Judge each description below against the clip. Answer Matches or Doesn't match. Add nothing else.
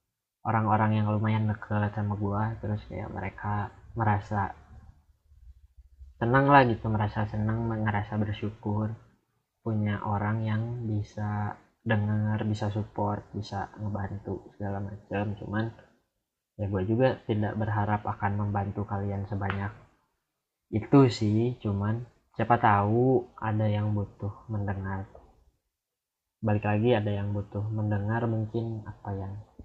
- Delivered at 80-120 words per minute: Matches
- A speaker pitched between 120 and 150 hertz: Doesn't match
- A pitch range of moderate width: Doesn't match